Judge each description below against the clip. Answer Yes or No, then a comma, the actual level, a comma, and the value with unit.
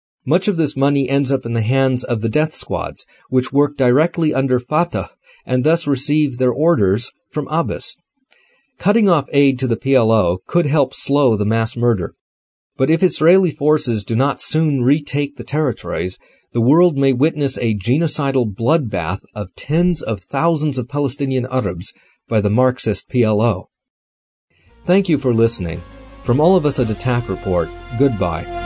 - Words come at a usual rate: Yes, average, 160 wpm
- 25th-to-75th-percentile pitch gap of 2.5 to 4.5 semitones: No, average, 5.0 semitones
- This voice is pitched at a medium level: No, low, 130 Hz